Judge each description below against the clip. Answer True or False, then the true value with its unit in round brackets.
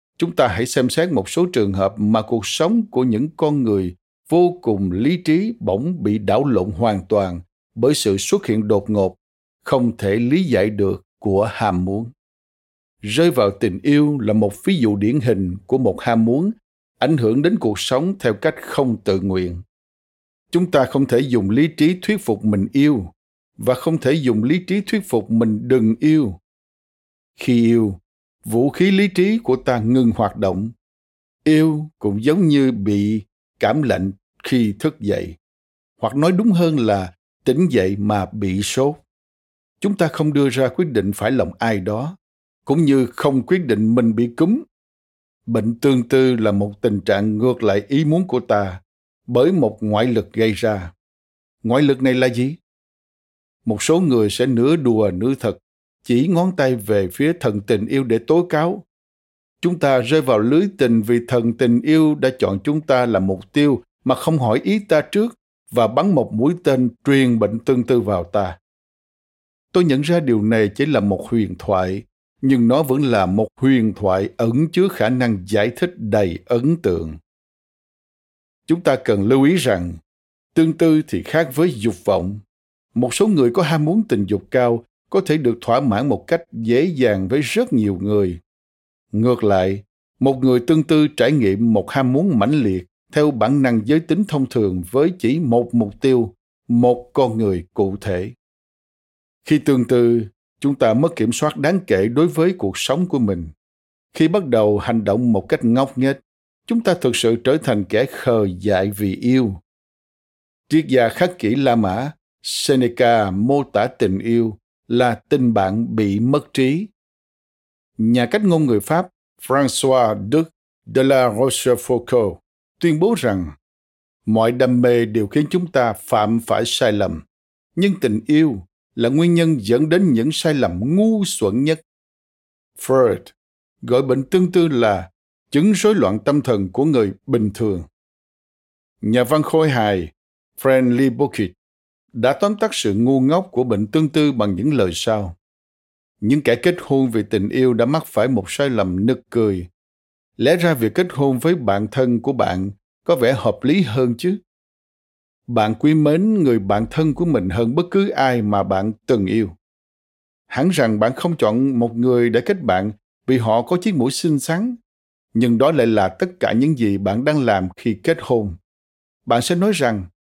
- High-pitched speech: False (120 Hz)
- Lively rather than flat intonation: True (6.7 semitones)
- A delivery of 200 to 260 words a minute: False (180 wpm)